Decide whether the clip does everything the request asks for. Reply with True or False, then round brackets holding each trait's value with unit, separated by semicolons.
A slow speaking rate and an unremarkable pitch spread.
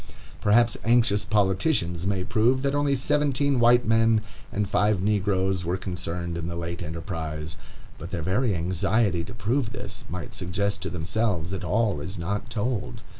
False (160 wpm; 4.8 semitones)